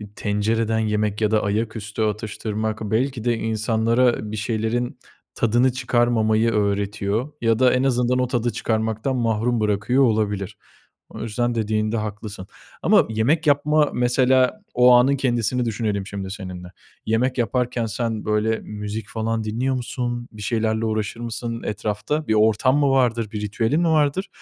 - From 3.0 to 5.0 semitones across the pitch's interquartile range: No, narrow, 2.5 semitones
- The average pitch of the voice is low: Yes, low, 115 Hz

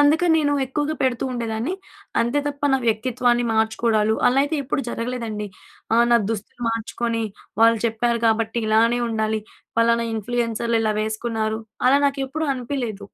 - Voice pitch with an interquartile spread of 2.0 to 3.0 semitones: Yes, narrow, 2.6 semitones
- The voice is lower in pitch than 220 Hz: No, high, 235 Hz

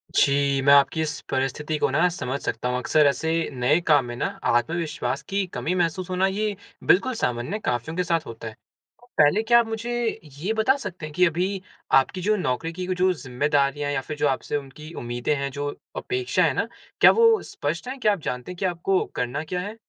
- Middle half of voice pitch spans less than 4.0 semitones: No, wide, 5.4 semitones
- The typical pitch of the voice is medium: Yes, medium, 160 Hz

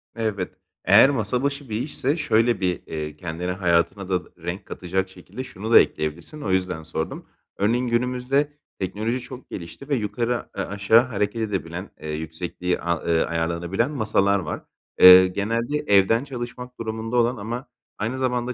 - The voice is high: No, low, 105 Hz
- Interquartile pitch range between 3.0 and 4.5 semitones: No, average, 5.3 semitones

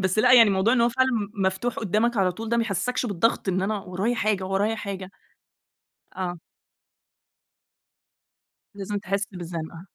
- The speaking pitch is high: Yes, high, 200 Hz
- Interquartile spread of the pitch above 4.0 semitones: No, average, 3.2 semitones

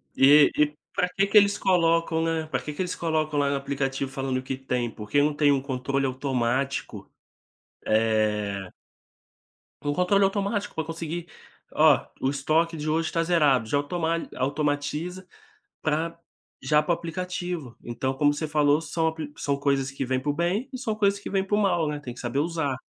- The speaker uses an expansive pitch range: No, average, 3.8 semitones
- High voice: No, medium, 150 Hz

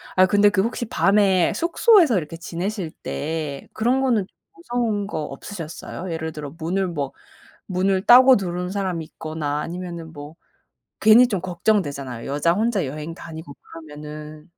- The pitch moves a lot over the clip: No, average, 4.9 semitones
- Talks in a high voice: No, medium, 175 Hz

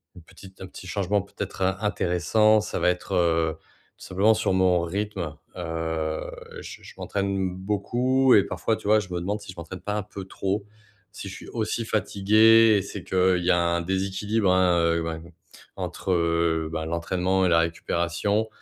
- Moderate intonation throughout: Yes, average, 3.2 semitones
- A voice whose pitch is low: Yes, very low, 95 Hz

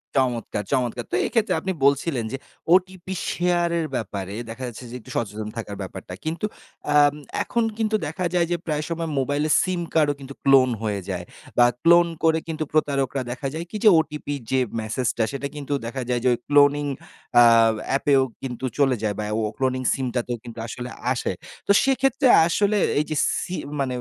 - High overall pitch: No, medium, 140 Hz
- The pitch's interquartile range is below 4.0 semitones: No, wide, 5.4 semitones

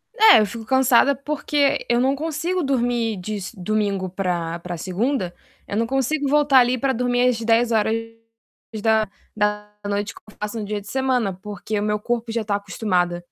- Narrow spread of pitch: No, average, 3.8 semitones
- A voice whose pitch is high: Yes, high, 225 Hz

